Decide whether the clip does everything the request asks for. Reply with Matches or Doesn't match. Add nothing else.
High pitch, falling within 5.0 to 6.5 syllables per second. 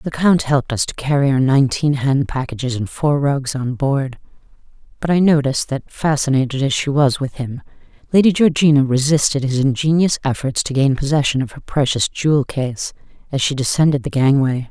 Doesn't match